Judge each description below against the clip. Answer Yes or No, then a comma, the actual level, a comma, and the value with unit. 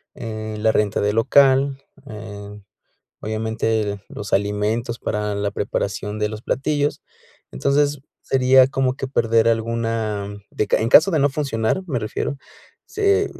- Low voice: Yes, low, 115 Hz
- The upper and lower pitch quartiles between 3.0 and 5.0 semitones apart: Yes, average, 4.1 semitones